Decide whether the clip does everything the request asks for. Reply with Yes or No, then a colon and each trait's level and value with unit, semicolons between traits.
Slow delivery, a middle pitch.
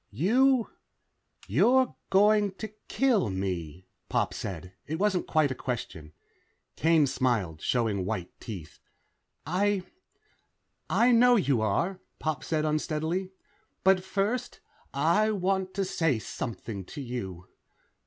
Yes: slow, 115 wpm; medium, 155 Hz